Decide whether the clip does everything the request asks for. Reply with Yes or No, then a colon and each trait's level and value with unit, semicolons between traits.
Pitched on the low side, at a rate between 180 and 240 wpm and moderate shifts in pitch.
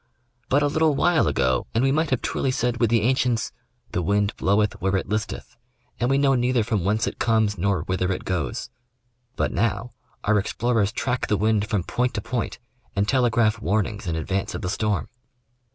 Yes: low, 110 Hz; average, 200 wpm; average, 3.7 semitones